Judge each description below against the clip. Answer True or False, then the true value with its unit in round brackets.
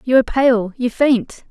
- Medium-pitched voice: False (245 Hz)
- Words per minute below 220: True (200 wpm)